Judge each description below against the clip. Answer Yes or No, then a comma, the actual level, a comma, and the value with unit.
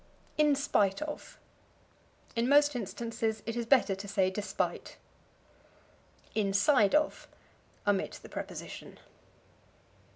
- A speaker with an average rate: No, slow, 100 wpm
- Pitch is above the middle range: Yes, high, 230 Hz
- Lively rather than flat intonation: Yes, wide, 5.8 semitones